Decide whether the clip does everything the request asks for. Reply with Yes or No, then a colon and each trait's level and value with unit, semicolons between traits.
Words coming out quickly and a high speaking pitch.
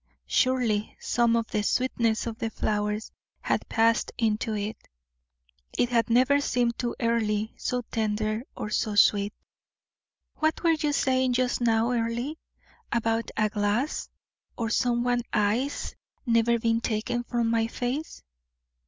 No: slow, 135 wpm; high, 230 Hz